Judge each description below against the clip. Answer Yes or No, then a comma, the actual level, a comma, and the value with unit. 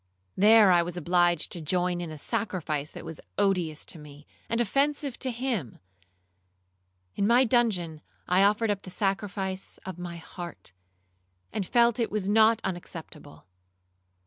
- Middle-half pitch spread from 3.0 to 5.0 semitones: No, wide, 5.6 semitones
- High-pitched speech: No, medium, 180 Hz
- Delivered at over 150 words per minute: No, average, 145 wpm